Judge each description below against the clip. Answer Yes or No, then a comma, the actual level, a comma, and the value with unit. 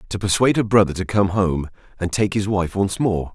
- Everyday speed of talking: No, fast, 235 wpm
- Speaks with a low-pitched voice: Yes, very low, 95 Hz